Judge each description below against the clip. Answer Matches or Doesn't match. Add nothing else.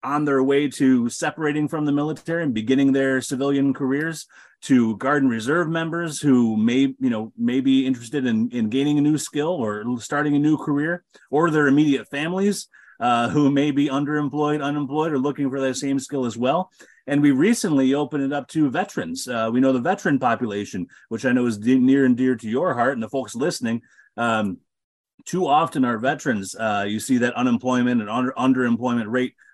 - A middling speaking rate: Matches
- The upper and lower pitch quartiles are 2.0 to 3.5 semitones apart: Matches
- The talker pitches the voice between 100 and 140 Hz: Matches